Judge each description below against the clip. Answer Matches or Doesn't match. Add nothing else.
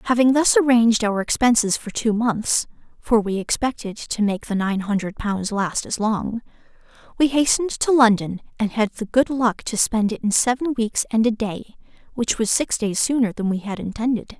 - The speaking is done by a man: Doesn't match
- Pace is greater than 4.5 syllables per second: Doesn't match